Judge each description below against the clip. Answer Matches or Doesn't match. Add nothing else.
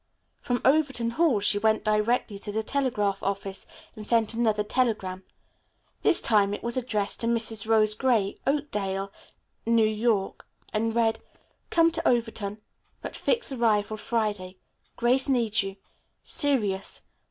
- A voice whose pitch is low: Doesn't match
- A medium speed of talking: Doesn't match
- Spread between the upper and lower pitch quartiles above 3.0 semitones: Doesn't match